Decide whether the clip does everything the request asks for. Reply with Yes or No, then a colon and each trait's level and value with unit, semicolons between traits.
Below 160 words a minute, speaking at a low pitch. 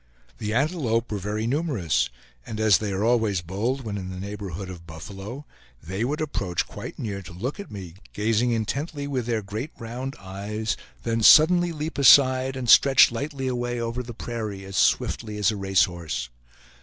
No: average, 175 wpm; low, 110 Hz